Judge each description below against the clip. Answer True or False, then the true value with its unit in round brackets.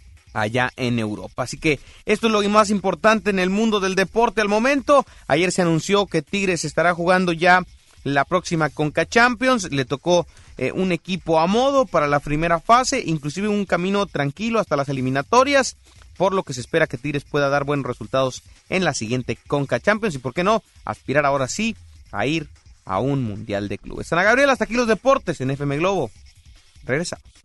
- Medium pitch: True (165 Hz)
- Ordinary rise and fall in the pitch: False (7.7 semitones)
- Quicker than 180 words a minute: True (190 wpm)